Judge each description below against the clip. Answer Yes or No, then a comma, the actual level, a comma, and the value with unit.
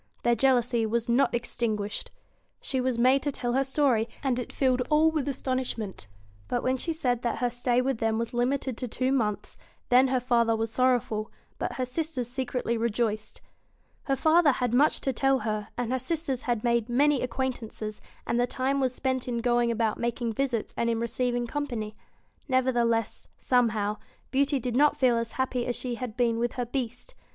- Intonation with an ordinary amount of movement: No, narrow, 2.0 semitones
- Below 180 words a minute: No, average, 190 wpm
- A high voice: Yes, high, 245 Hz